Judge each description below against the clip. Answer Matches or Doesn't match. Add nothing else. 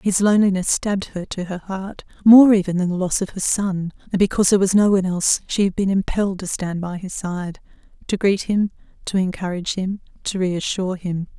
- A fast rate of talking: Matches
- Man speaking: Doesn't match